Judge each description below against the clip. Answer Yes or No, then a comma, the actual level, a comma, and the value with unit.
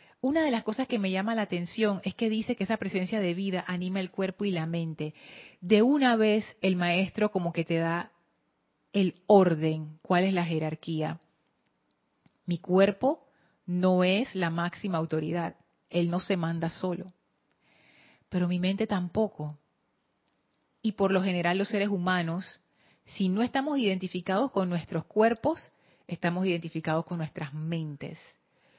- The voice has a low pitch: No, medium, 185 Hz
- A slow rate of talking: No, average, 150 wpm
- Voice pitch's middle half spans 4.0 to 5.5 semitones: No, average, 3.5 semitones